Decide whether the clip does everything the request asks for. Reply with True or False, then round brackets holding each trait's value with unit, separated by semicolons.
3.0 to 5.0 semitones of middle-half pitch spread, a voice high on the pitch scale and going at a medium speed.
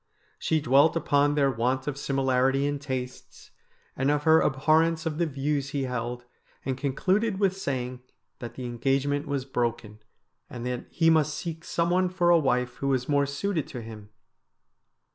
False (3.8 semitones; 140 Hz; 175 wpm)